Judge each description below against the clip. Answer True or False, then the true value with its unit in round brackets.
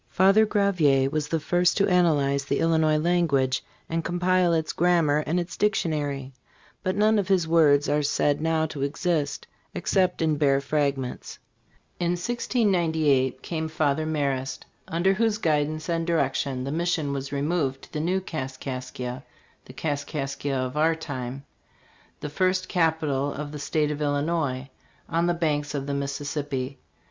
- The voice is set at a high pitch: False (155 Hz)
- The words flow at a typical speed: True (150 wpm)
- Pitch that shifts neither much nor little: True (3.5 semitones)